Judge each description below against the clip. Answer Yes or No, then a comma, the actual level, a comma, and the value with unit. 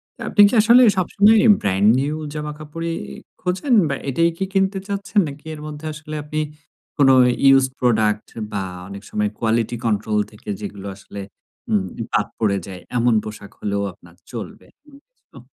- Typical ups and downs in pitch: No, wide, 7.9 semitones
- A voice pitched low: Yes, low, 130 Hz